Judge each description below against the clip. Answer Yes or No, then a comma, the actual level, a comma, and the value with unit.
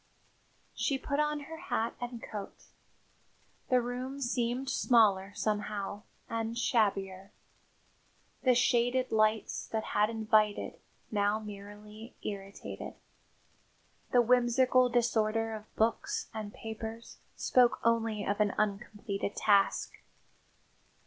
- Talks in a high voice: Yes, high, 225 Hz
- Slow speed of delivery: Yes, slow, 105 wpm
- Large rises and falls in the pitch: No, average, 2.7 semitones